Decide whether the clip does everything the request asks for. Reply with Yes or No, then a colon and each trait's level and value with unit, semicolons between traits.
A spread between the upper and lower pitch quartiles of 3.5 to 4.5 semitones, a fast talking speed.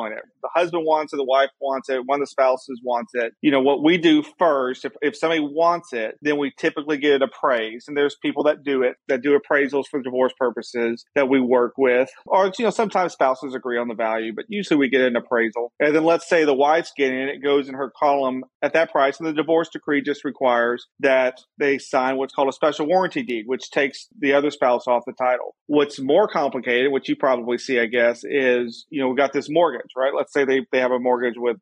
No: average, 2.7 semitones; fast, 240 wpm